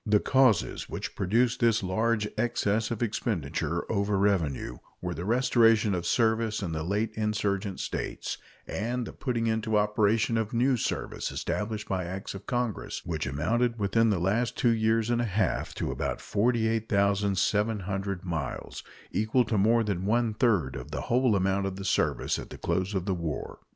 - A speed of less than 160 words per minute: No, average, 170 wpm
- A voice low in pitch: Yes, low, 105 Hz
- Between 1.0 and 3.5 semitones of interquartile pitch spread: Yes, average, 3.0 semitones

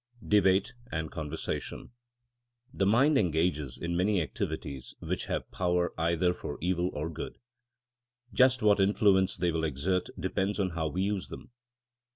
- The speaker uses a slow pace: No, average, 150 wpm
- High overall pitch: No, very low, 90 Hz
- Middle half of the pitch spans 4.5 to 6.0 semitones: No, average, 3.4 semitones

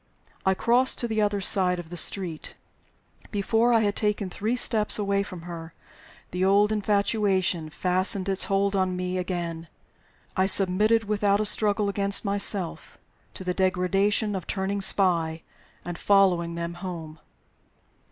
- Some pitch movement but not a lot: No, narrow, 2.3 semitones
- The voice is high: Yes, high, 195 Hz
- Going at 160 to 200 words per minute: No, average, 145 wpm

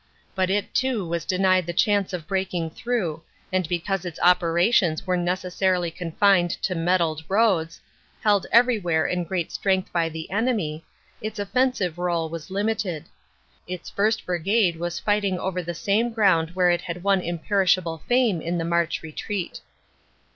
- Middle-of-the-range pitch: Yes, medium, 180 Hz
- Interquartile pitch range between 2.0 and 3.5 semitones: Yes, average, 3.0 semitones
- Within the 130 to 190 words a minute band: Yes, average, 155 wpm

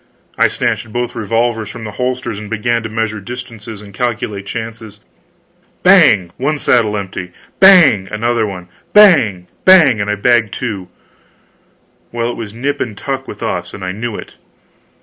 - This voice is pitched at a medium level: No, low, 110 Hz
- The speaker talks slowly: No, average, 160 wpm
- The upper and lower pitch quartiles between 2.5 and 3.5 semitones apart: Yes, average, 2.9 semitones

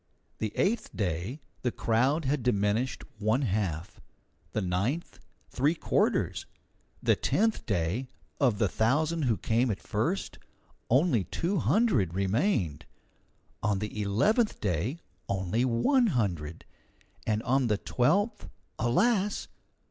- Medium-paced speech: No, slow, 120 wpm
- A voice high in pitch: No, low, 115 Hz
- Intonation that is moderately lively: No, wide, 7.1 semitones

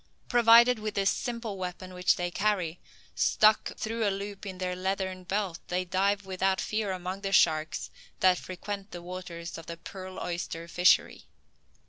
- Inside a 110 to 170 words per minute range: Yes, average, 160 wpm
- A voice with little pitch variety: Yes, narrow, 2.3 semitones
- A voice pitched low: No, high, 190 Hz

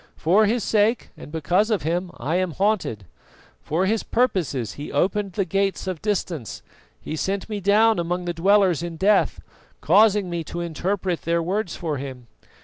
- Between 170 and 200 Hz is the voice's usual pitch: Yes, medium, 185 Hz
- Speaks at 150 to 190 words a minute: Yes, average, 175 wpm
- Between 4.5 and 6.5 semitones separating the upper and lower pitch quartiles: No, average, 3.7 semitones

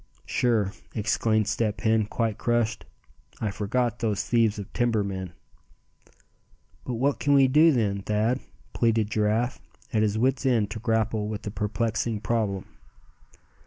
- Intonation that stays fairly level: Yes, narrow, 2.2 semitones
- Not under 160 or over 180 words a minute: No, average, 140 wpm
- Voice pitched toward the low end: Yes, low, 110 Hz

